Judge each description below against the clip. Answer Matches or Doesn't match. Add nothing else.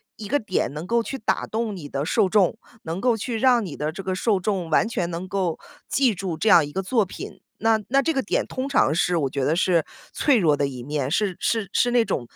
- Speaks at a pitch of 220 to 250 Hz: Doesn't match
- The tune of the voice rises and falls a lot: Matches